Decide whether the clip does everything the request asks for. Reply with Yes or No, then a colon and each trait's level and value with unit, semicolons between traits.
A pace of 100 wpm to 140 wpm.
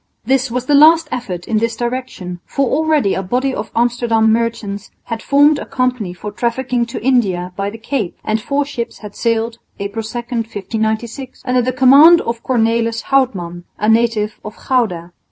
No: average, 170 wpm